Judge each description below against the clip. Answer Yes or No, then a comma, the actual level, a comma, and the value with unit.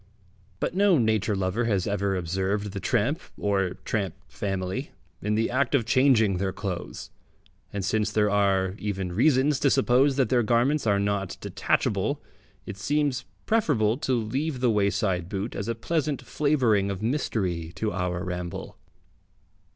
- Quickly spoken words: No, average, 150 wpm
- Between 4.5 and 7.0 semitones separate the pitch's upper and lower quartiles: Yes, average, 4.9 semitones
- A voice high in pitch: No, low, 105 Hz